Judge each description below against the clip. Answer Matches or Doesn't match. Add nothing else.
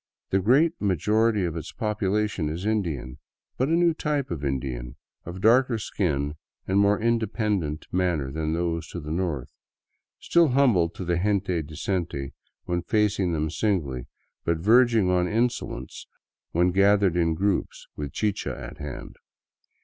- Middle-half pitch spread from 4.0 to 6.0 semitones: Matches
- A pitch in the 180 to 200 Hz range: Doesn't match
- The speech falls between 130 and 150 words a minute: Matches